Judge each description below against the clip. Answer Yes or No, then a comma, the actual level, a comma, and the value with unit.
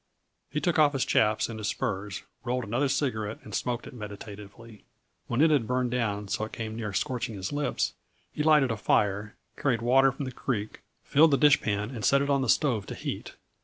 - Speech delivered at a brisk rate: Yes, fast, 210 wpm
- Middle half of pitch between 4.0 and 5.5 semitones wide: Yes, average, 4.3 semitones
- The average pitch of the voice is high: No, low, 120 Hz